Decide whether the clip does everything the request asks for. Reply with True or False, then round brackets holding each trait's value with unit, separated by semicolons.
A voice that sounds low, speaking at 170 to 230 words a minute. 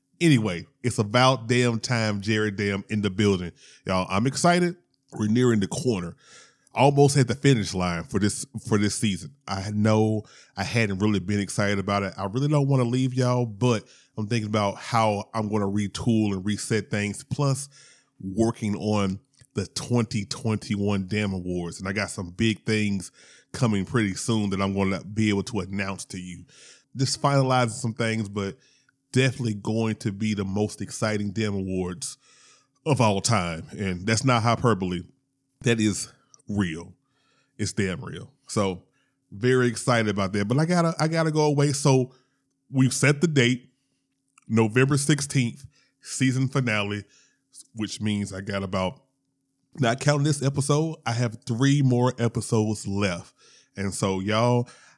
False (110 Hz; 160 wpm)